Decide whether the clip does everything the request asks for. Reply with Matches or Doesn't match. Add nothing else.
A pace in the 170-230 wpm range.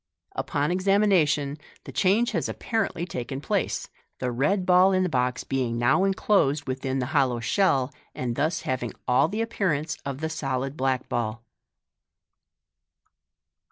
Doesn't match